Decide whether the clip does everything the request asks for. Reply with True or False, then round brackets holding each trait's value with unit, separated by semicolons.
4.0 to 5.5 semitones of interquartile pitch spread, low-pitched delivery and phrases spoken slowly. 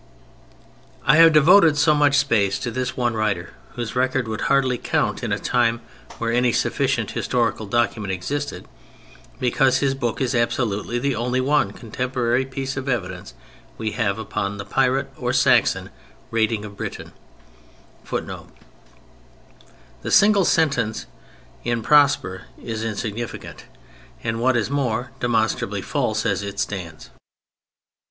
False (3.6 semitones; 120 Hz; 130 wpm)